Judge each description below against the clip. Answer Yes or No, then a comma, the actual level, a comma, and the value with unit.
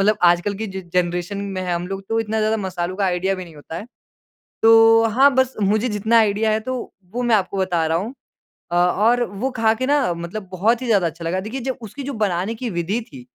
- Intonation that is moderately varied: Yes, average, 4.0 semitones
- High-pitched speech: Yes, high, 205 Hz